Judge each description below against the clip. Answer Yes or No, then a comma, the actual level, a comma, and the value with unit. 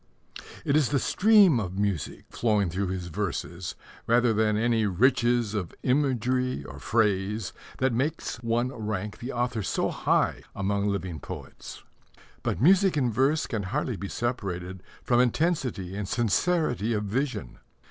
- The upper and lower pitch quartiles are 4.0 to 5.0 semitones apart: Yes, average, 4.4 semitones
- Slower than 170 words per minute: Yes, average, 145 wpm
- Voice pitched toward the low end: Yes, low, 115 Hz